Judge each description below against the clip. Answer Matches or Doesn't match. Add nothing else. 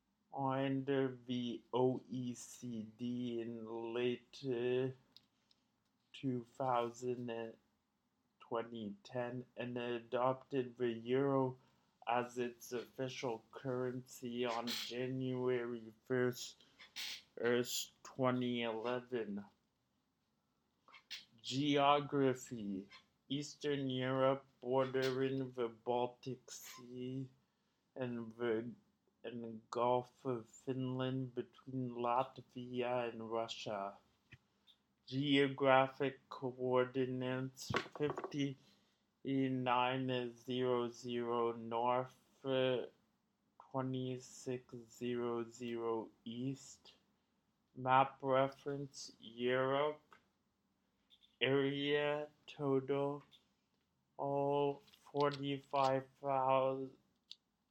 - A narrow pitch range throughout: Matches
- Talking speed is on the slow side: Matches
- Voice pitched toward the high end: Doesn't match